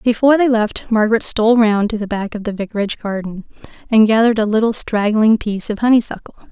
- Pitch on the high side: Yes, high, 220 Hz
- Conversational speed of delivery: Yes, average, 195 wpm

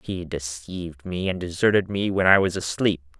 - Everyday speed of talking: Yes, average, 190 wpm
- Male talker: Yes, male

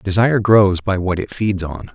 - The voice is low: Yes, low, 100 Hz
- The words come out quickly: Yes, fast, 215 wpm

